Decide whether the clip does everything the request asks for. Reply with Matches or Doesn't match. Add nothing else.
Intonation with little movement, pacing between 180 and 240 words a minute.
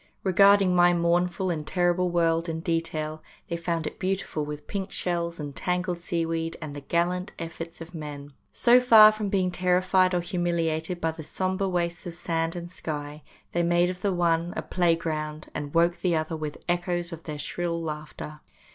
Matches